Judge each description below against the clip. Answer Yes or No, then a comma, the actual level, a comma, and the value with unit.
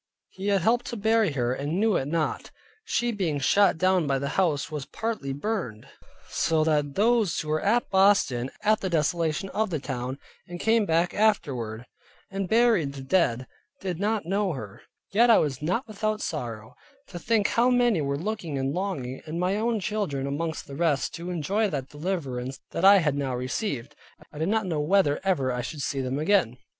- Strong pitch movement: Yes, wide, 6.7 semitones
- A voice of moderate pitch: Yes, medium, 170 Hz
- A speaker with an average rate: Yes, average, 195 wpm